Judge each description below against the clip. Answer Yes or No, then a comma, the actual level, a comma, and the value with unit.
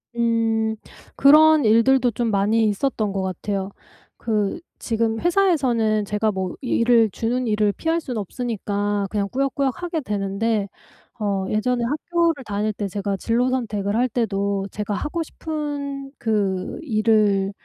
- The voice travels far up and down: No, average, 4.1 semitones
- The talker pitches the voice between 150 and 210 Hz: No, high, 225 Hz